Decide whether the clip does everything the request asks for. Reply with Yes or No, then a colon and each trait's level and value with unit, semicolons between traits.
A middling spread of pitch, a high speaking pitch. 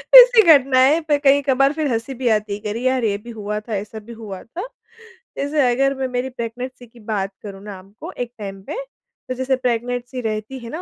Yes: average, 3.8 semitones; high, 245 Hz